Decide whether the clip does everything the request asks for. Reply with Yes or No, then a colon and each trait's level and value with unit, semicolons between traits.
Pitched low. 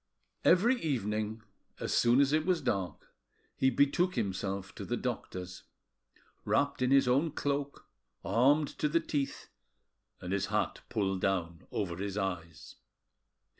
Yes: low, 110 Hz